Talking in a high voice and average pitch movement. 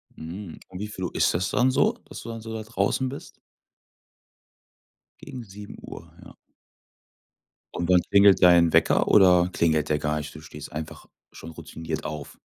No: very low, 90 Hz; average, 4.8 semitones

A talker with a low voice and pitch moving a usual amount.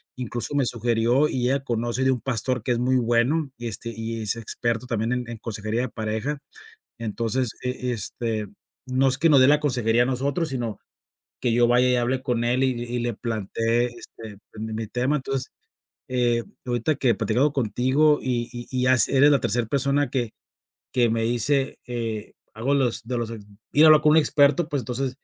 No: low, 125 Hz; narrow, 2.3 semitones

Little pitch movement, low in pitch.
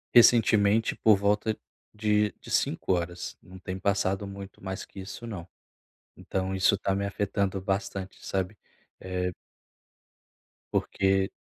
Yes: narrow, 1.5 semitones; low, 100 Hz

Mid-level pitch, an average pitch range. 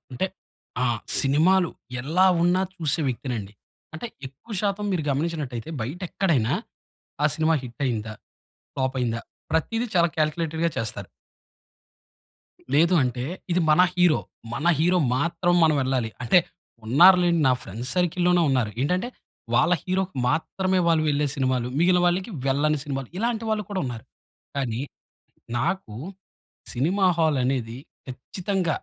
No: medium, 155 Hz; wide, 5.7 semitones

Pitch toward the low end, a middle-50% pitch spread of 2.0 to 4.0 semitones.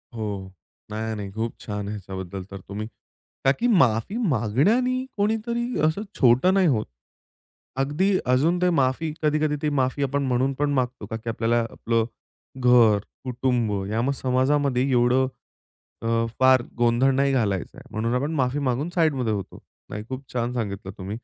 No: low, 125 Hz; average, 4.6 semitones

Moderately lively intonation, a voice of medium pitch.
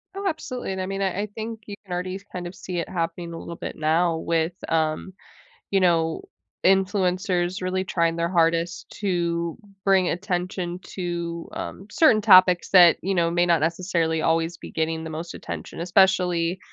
No: narrow, 2.1 semitones; medium, 175 Hz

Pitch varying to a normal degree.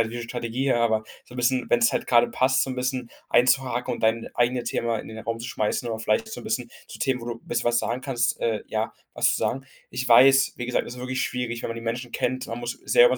No: narrow, 1.6 semitones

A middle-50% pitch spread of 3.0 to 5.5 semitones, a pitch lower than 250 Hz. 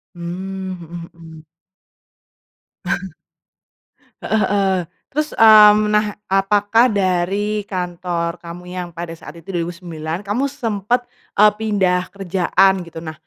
Yes: average, 3.3 semitones; high, 190 Hz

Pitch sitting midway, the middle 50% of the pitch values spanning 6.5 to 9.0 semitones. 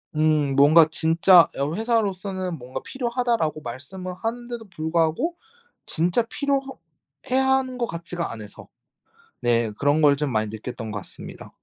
Yes: medium, 165 Hz; wide, 8.4 semitones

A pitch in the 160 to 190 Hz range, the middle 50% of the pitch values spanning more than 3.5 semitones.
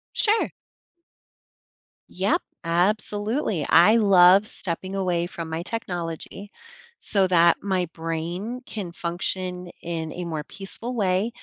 No: medium, 185 Hz; average, 3.2 semitones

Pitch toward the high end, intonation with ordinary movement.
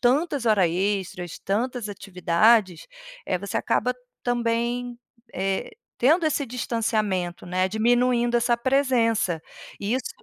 Yes: high, 230 Hz; average, 4.2 semitones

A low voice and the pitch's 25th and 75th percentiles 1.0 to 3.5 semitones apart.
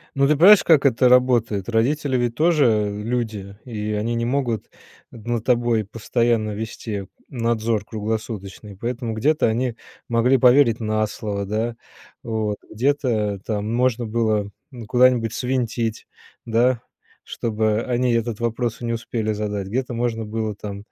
Yes: low, 115 Hz; narrow, 2.4 semitones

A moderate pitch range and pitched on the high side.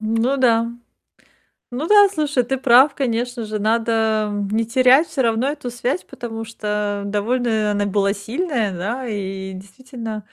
Yes: average, 3.5 semitones; high, 230 Hz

